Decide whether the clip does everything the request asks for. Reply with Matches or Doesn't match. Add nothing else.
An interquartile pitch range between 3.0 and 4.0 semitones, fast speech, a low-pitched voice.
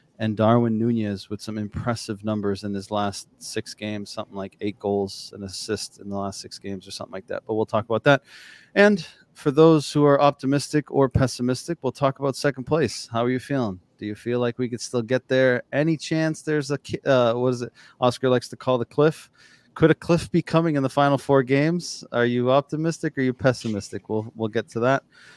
Doesn't match